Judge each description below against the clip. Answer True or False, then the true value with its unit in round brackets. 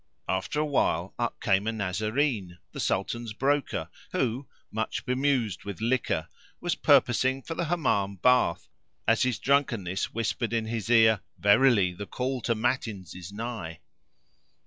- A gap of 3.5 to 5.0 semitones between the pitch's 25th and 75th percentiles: True (4.3 semitones)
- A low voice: True (115 Hz)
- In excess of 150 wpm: False (145 wpm)